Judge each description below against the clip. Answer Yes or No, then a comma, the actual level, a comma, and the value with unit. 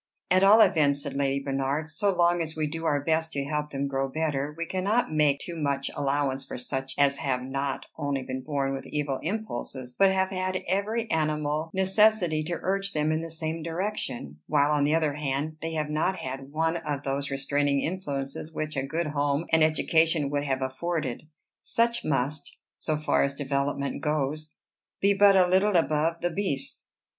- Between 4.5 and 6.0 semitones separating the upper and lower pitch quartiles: No, average, 3.3 semitones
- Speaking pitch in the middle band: Yes, medium, 150 Hz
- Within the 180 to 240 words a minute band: Yes, average, 190 wpm